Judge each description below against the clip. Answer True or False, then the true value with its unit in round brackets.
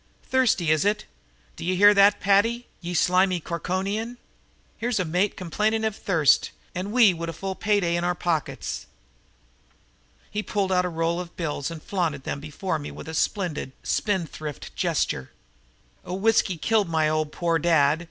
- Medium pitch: True (180 Hz)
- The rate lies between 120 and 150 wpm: False (165 wpm)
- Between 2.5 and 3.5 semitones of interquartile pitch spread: False (3.9 semitones)